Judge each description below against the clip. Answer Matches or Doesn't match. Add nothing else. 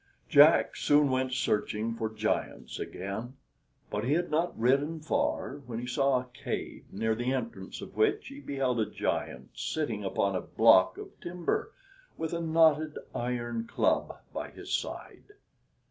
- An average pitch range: Doesn't match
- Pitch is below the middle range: Matches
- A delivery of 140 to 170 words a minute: Matches